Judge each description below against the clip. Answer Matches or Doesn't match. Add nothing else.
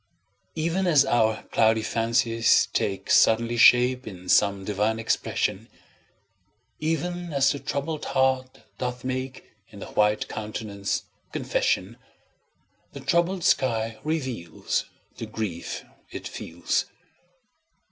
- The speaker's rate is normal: Doesn't match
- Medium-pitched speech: Doesn't match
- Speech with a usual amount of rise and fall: Matches